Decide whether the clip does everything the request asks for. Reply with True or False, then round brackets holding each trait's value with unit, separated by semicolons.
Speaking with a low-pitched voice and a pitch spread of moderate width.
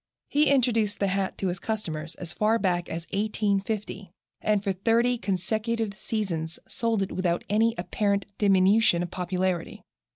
False (200 Hz; 3.2 semitones)